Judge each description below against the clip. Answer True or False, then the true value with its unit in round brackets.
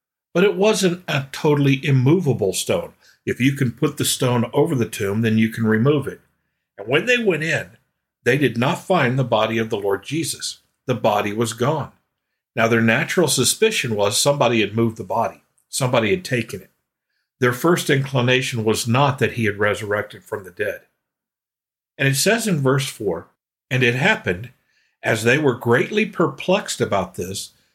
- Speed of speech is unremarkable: True (175 wpm)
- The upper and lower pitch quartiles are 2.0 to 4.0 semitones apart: False (5.2 semitones)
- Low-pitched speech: True (130 Hz)